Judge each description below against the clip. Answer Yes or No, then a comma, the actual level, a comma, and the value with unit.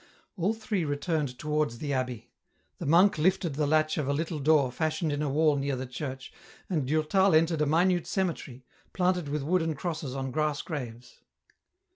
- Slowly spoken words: No, average, 175 wpm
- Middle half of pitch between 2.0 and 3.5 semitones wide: Yes, average, 3.2 semitones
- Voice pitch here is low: No, medium, 150 Hz